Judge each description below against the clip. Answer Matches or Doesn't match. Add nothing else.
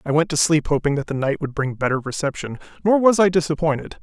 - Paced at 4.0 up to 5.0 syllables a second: Doesn't match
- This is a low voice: Doesn't match